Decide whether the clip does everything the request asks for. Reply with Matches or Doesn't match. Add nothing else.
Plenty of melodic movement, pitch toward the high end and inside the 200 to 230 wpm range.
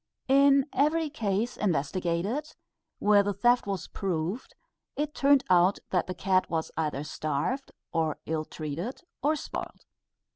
Doesn't match